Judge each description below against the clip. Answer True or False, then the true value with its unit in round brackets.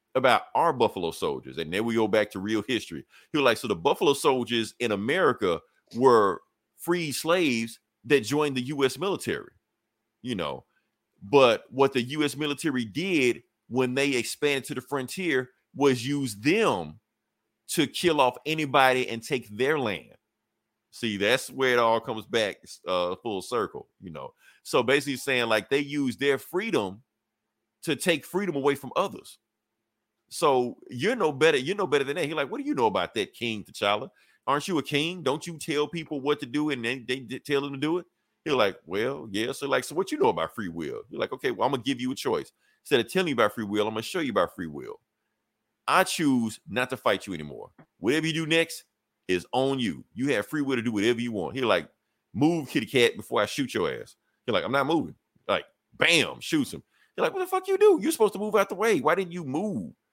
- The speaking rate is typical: False (215 wpm)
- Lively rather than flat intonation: True (7.9 semitones)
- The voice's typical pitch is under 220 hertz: True (140 Hz)